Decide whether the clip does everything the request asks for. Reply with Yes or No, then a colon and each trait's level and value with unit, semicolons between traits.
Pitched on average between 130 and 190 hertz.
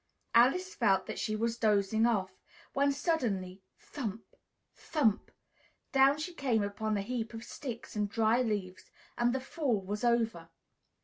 No: high, 225 Hz